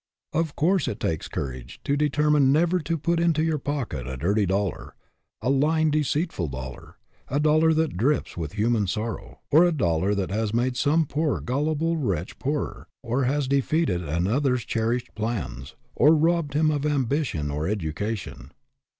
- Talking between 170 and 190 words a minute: No, average, 160 wpm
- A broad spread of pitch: Yes, wide, 7.5 semitones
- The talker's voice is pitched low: Yes, low, 130 Hz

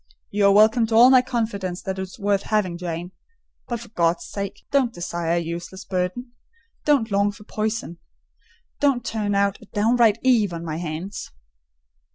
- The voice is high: Yes, high, 200 Hz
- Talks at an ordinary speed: Yes, average, 165 wpm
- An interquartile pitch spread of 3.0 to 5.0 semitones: Yes, average, 4.1 semitones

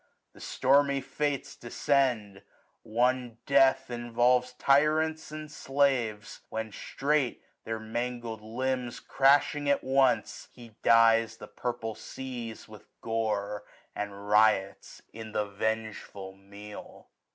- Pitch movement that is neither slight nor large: Yes, average, 3.5 semitones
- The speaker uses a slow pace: Yes, slow, 105 wpm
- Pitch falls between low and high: No, low, 120 Hz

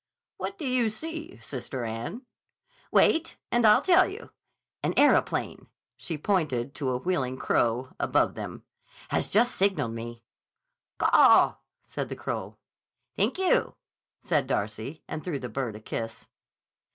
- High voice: No, medium, 145 Hz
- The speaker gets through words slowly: Yes, slow, 130 wpm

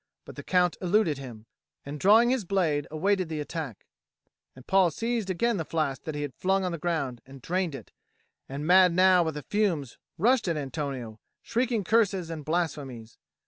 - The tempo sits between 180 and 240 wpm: Yes, average, 185 wpm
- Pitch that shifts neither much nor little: Yes, average, 4.9 semitones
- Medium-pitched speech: Yes, medium, 170 Hz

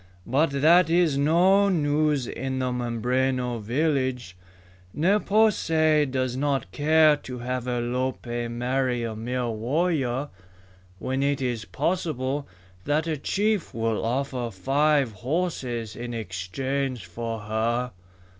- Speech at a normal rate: No, slow, 120 wpm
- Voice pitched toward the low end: Yes, low, 130 Hz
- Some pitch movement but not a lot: Yes, average, 4.1 semitones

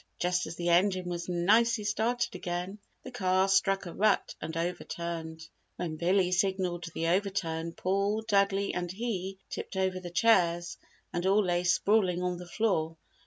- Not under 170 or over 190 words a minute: No, average, 160 wpm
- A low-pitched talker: No, medium, 185 Hz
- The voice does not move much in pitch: Yes, narrow, 2.3 semitones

